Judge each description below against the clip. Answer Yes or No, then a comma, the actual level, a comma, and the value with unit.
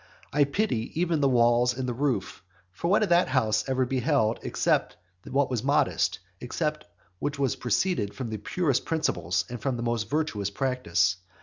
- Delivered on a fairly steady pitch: No, average, 4.2 semitones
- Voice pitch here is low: Yes, low, 125 Hz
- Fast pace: No, average, 170 wpm